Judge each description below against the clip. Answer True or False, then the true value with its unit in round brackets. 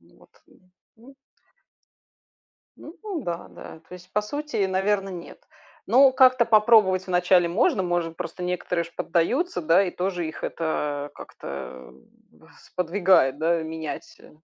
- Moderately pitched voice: True (180 Hz)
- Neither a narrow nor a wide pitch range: True (4.0 semitones)